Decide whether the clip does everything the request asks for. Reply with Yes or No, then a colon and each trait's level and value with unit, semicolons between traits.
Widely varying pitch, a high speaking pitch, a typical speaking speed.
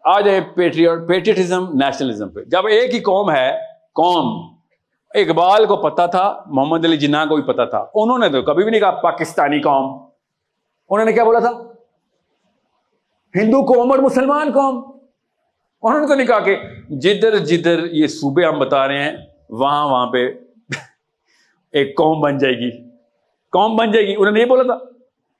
Yes: wide, 8.0 semitones; high, 195 Hz; average, 170 wpm